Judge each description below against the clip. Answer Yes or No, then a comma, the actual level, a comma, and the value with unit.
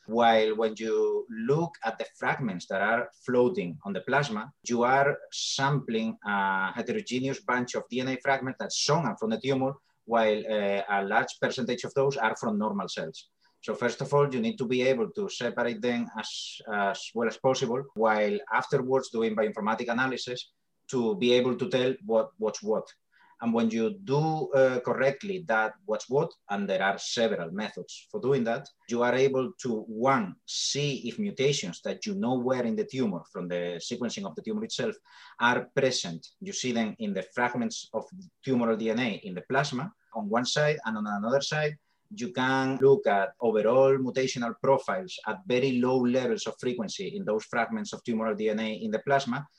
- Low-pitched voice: Yes, low, 125 Hz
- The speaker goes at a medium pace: Yes, average, 180 wpm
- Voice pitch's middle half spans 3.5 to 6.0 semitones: Yes, average, 3.9 semitones